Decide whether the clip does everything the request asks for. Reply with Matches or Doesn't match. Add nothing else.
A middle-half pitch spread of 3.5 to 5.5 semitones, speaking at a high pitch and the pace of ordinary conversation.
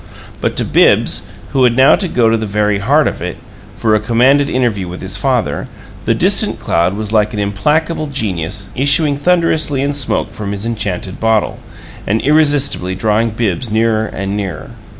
Doesn't match